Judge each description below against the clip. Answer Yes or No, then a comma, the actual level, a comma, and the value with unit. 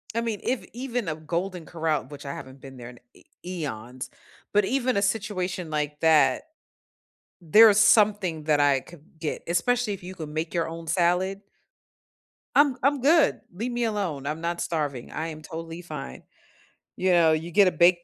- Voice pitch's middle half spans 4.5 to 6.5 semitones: Yes, average, 4.9 semitones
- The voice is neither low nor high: Yes, medium, 170 Hz